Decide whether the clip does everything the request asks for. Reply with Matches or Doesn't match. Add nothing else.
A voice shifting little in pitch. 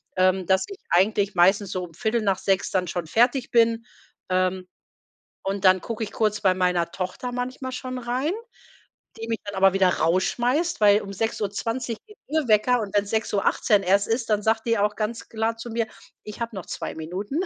Doesn't match